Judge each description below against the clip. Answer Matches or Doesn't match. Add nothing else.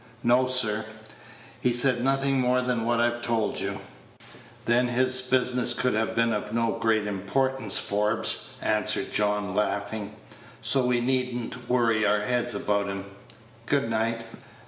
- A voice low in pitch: Matches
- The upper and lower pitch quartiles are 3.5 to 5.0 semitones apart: Doesn't match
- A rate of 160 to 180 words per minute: Doesn't match